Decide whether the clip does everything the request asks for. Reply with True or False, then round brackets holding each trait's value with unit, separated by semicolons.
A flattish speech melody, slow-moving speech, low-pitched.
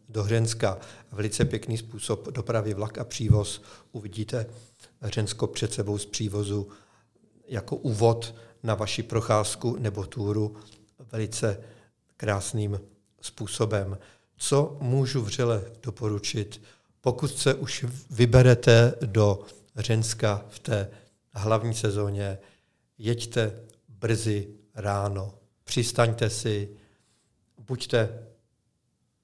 True (2.2 semitones; 90 wpm; 110 Hz)